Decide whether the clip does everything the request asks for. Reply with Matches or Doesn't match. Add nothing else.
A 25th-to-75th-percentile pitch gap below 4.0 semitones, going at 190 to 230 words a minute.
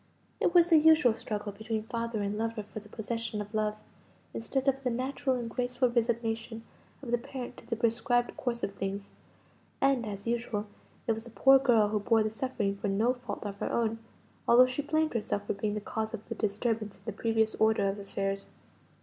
Matches